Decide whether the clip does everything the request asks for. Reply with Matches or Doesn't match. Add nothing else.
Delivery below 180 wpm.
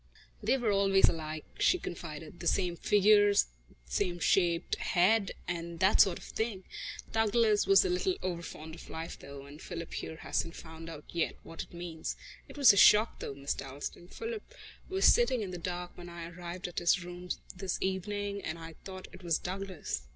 Doesn't match